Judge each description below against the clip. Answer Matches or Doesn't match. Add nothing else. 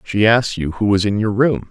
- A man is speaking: Matches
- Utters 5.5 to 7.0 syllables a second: Matches